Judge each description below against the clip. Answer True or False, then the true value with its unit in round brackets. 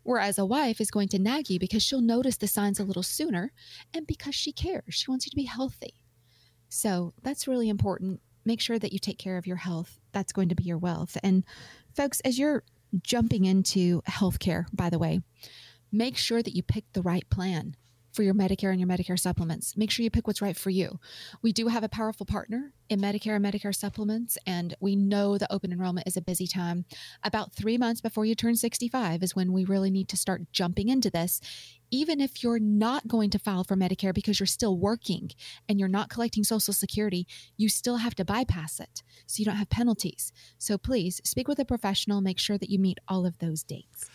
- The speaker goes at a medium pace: False (220 wpm)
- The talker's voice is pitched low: False (200 Hz)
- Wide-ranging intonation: False (3.7 semitones)